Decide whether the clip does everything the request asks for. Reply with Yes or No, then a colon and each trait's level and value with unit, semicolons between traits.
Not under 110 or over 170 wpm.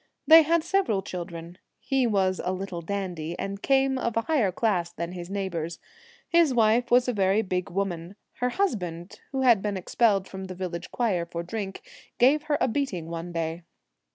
No: average, 180 wpm